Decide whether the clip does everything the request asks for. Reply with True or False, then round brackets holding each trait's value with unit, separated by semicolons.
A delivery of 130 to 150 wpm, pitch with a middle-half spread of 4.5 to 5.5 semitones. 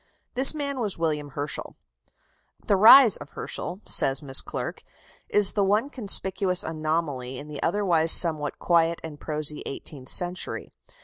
True (140 wpm; 5.1 semitones)